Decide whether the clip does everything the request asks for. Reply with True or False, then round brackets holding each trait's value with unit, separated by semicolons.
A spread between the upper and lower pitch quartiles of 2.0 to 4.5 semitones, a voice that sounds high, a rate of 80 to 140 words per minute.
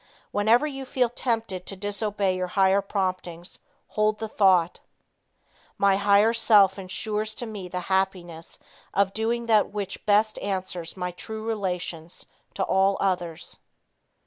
True (2.8 semitones; 200 Hz; 135 wpm)